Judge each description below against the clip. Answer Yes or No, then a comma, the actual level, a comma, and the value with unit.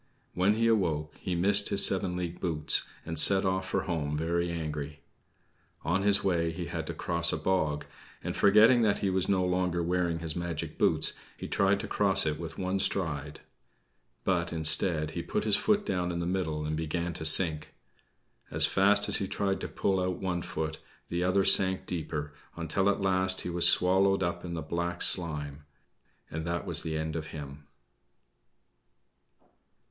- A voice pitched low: Yes, very low, 85 Hz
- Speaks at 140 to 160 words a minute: No, average, 180 wpm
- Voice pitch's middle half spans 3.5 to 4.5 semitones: No, average, 3.1 semitones